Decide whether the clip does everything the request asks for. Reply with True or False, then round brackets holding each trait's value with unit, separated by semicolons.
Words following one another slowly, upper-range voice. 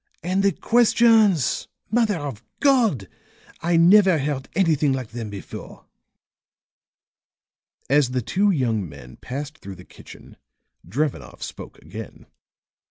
False (115 wpm; 145 Hz)